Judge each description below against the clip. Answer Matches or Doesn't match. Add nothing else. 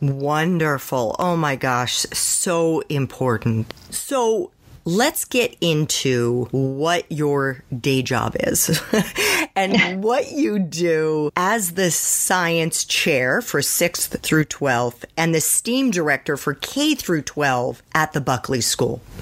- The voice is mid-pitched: Matches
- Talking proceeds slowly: Matches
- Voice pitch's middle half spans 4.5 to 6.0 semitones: Matches